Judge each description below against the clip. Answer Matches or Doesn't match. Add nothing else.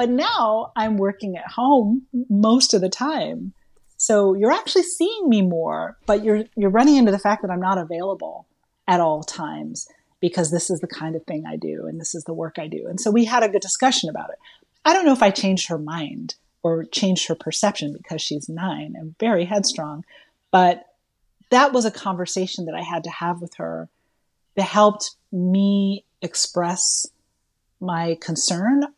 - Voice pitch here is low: Doesn't match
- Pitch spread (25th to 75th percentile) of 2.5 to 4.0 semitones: Doesn't match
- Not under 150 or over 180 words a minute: Doesn't match